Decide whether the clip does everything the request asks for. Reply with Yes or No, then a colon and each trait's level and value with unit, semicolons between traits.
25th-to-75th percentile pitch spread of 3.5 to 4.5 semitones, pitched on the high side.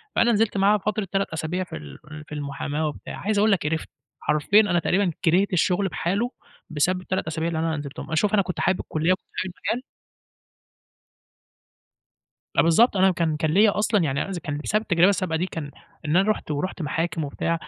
No: average, 4.0 semitones; medium, 175 Hz